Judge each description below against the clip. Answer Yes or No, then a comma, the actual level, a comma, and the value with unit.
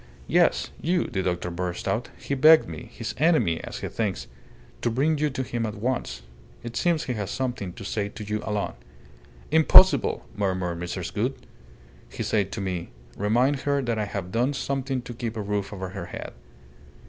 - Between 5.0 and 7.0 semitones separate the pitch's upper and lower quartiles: Yes, wide, 5.5 semitones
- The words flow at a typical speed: Yes, average, 185 wpm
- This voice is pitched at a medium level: No, low, 110 Hz